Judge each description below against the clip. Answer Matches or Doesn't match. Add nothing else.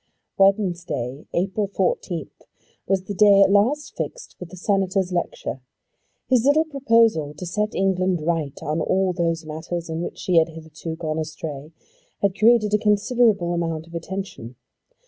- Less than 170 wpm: Matches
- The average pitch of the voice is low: Doesn't match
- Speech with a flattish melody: Doesn't match